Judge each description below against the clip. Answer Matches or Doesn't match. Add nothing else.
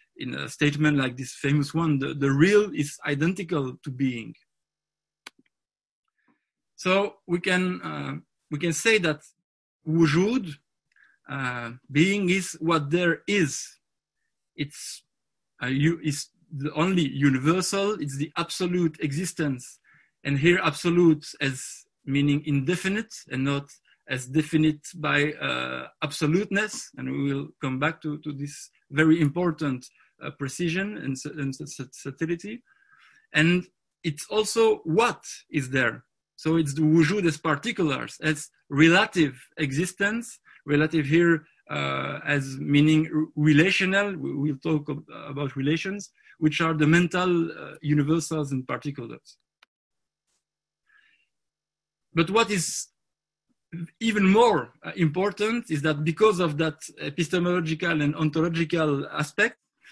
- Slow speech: Matches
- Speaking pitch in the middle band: Matches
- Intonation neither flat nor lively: Matches